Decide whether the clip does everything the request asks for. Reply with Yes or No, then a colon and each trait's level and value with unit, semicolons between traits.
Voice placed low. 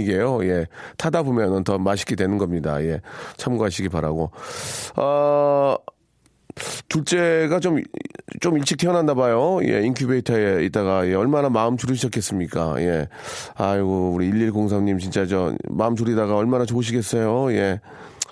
Yes: low, 110 Hz